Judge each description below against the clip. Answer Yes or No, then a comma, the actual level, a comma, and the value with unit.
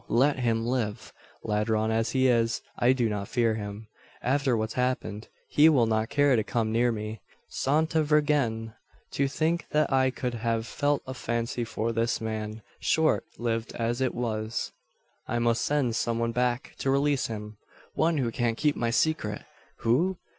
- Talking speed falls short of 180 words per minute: Yes, average, 170 wpm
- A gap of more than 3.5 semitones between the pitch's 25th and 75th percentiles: No, average, 3.2 semitones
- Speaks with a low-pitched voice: Yes, low, 120 Hz